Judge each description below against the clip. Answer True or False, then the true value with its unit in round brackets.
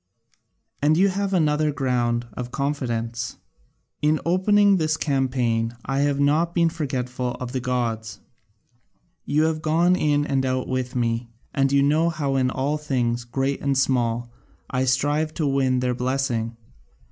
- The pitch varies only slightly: False (3.5 semitones)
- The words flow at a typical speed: True (150 wpm)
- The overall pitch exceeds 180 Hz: False (135 Hz)